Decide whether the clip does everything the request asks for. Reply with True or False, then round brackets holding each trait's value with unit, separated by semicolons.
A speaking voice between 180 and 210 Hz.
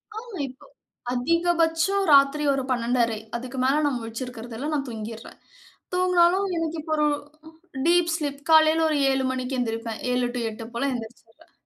False (275 Hz)